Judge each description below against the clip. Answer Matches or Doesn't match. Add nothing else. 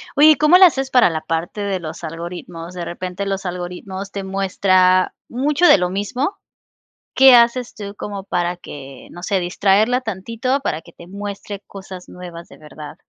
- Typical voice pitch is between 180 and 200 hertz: Matches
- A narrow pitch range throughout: Doesn't match